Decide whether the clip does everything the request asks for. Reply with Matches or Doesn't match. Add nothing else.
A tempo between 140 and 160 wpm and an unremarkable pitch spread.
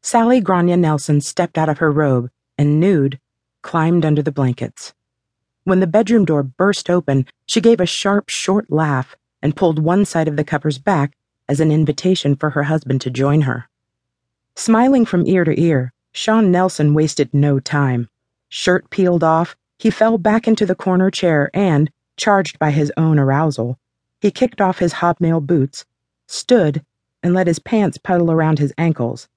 Doesn't match